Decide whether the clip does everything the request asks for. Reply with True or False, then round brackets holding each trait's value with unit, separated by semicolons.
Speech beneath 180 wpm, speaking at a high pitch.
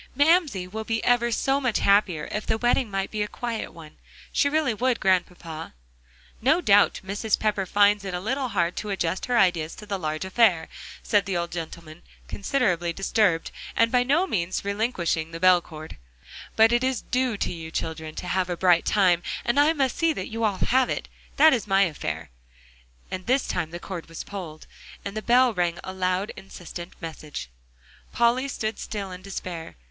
False (190 wpm; 195 Hz)